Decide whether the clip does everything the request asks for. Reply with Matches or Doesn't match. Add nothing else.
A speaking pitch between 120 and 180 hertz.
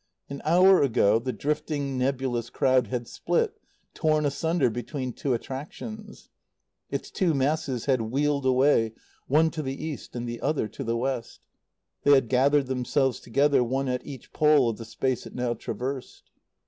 Matches